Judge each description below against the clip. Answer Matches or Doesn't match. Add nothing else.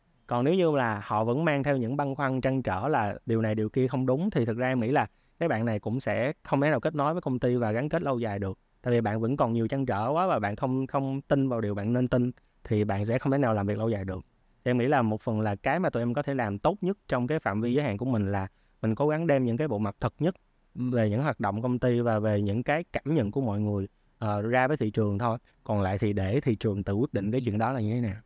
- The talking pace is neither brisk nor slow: Doesn't match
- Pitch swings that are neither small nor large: Matches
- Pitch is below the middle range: Matches